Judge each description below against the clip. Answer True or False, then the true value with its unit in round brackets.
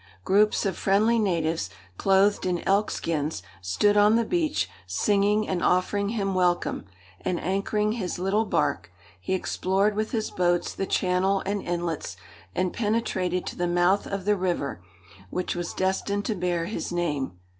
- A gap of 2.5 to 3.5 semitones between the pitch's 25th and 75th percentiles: True (2.9 semitones)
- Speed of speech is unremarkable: True (155 wpm)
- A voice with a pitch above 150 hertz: True (190 Hz)